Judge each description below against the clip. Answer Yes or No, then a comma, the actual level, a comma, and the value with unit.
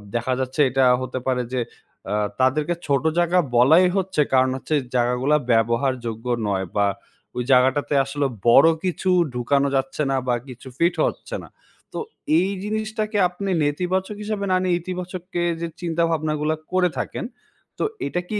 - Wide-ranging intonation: Yes, wide, 5.9 semitones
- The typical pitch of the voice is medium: Yes, medium, 150 Hz